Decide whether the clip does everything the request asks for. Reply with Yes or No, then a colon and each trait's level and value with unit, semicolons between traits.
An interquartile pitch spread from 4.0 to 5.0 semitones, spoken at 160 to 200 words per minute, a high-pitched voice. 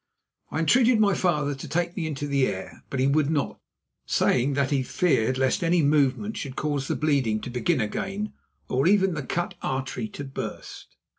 No: average, 4.7 semitones; average, 190 wpm; medium, 145 Hz